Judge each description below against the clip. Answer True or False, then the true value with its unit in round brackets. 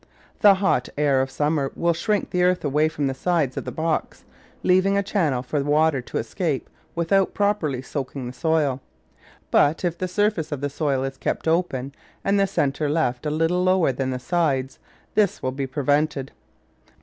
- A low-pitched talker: False (150 Hz)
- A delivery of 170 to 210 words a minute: True (185 wpm)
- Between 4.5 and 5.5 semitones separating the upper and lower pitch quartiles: True (4.8 semitones)